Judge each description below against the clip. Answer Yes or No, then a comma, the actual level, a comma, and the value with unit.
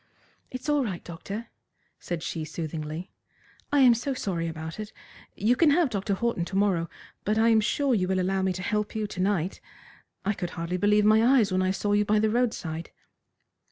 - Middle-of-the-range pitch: No, high, 205 Hz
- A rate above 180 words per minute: Yes, average, 200 wpm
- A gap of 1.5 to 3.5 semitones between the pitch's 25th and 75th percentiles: No, average, 4.0 semitones